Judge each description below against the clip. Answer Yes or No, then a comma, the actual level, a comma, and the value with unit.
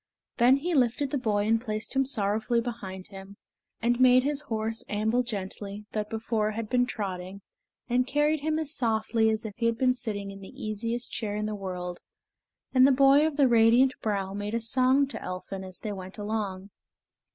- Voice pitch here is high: Yes, high, 225 Hz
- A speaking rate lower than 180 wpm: No, average, 195 wpm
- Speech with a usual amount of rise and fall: Yes, average, 3.7 semitones